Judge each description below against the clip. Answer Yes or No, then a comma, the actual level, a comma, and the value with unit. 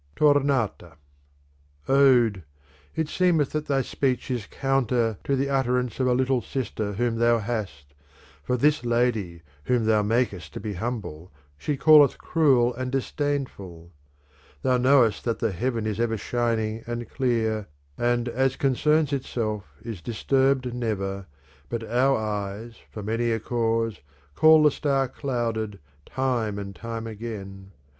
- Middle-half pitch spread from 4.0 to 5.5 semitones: No, average, 3.5 semitones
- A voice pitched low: Yes, low, 120 Hz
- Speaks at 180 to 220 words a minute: No, average, 145 wpm